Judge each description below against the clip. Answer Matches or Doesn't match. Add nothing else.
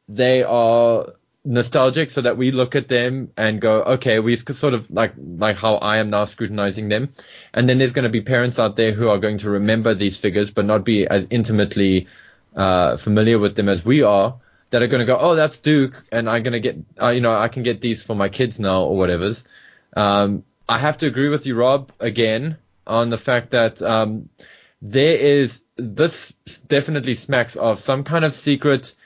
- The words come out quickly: Matches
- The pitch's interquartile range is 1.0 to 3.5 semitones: Matches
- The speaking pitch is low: Matches